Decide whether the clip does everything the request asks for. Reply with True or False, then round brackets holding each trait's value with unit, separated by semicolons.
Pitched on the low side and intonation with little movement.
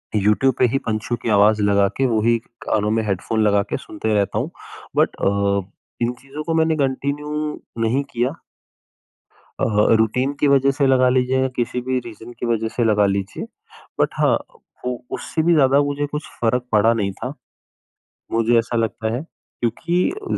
False (120 Hz; 4.1 semitones)